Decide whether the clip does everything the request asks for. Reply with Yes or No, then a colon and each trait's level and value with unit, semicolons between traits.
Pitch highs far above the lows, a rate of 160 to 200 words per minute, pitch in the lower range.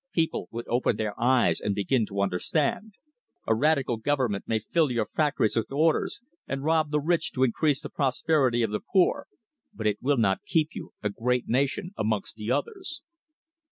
Yes: wide, 5.8 semitones; average, 180 wpm; low, 130 Hz